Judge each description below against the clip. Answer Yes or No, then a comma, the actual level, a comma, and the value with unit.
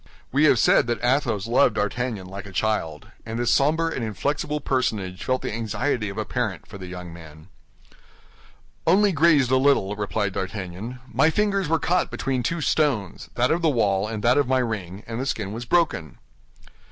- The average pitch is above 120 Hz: No, low, 115 Hz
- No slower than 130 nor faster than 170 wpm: No, average, 180 wpm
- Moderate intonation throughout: No, wide, 6.1 semitones